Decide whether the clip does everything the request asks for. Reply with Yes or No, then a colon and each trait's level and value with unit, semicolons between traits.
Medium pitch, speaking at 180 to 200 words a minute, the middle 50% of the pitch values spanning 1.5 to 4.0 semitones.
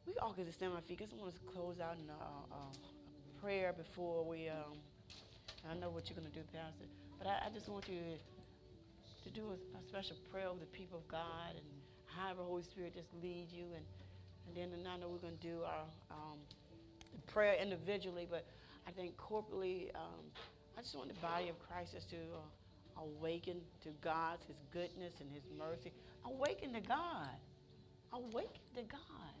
Yes: medium, 170 Hz; average, 190 wpm; average, 3.2 semitones